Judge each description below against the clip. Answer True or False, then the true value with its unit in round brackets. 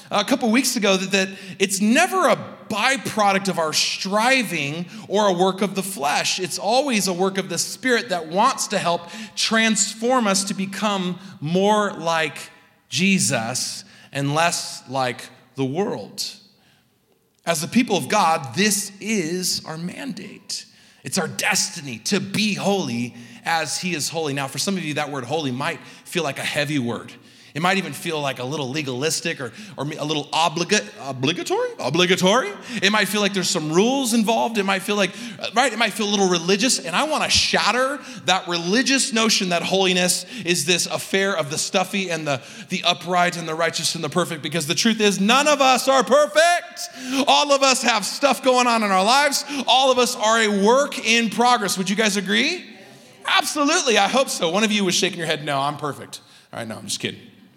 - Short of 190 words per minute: False (195 wpm)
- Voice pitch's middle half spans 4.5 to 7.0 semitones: True (4.9 semitones)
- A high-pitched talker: True (195 Hz)